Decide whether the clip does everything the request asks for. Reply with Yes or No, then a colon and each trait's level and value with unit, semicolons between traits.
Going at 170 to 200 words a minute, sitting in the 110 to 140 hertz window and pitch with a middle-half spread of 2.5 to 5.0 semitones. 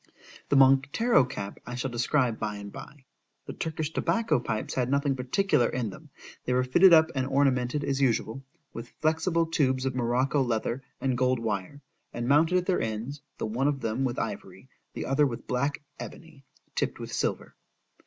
Yes: average, 175 wpm; low, 135 Hz; average, 3.1 semitones